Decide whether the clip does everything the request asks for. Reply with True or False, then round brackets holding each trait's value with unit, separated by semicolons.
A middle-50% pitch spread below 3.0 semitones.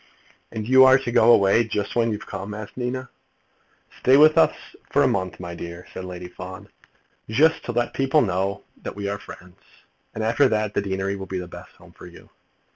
False (4.3 semitones)